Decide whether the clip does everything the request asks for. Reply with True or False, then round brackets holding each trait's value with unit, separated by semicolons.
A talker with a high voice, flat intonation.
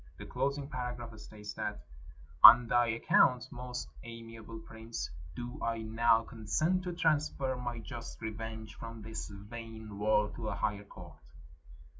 False (115 Hz; 2.0 semitones)